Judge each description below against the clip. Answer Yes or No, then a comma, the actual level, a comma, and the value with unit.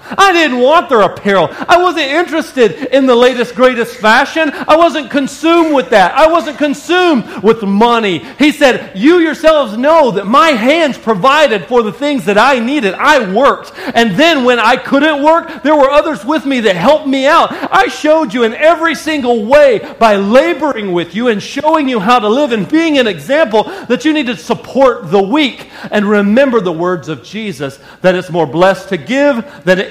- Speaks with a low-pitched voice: No, very high, 265 Hz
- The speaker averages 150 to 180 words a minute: No, average, 195 wpm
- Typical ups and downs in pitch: No, wide, 5.9 semitones